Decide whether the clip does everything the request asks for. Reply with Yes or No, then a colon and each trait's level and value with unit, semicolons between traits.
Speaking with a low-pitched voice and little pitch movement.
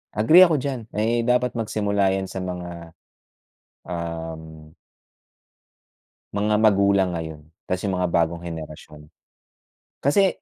No: very low, 95 Hz; average, 4.7 semitones